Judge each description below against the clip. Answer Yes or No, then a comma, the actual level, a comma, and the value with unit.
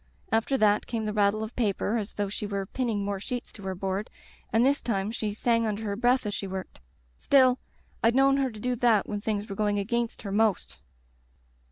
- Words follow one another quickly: Yes, fast, 215 wpm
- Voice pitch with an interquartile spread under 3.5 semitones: Yes, average, 2.8 semitones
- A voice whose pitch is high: Yes, high, 215 Hz